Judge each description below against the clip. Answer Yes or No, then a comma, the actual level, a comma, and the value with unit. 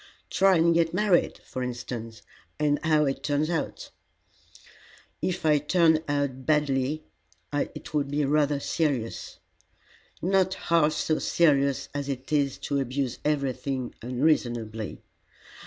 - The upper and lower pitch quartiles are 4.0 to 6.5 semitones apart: No, average, 3.0 semitones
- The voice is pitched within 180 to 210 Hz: No, medium, 145 Hz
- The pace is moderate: No, slow, 125 wpm